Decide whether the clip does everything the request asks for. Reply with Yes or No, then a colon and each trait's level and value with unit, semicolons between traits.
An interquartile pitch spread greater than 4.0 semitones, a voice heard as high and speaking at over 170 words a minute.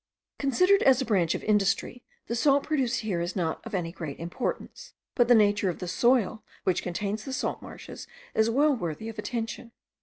Yes: average, 5.3 semitones; high, 220 Hz; average, 190 wpm